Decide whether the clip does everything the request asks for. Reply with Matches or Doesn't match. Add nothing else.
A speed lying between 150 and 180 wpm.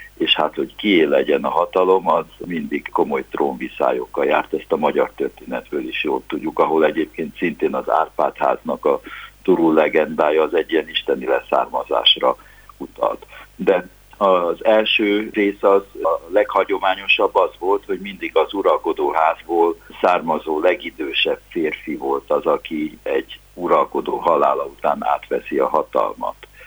Doesn't match